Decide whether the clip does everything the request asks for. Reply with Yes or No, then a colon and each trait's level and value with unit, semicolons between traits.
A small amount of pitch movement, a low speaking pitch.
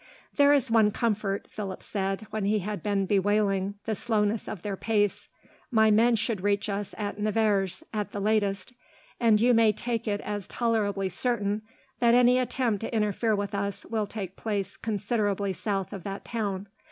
No: narrow, 2.0 semitones; high, 210 Hz